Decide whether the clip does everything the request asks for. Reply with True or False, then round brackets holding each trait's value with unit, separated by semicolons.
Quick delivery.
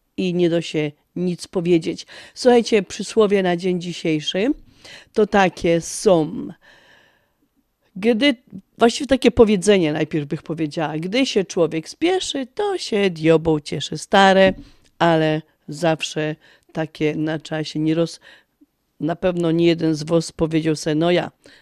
False (130 wpm)